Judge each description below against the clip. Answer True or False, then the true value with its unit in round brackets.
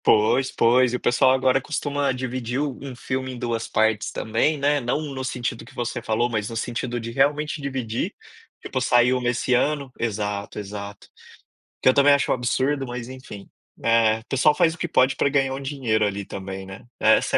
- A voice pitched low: True (125 Hz)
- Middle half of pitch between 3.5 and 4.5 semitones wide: False (3.1 semitones)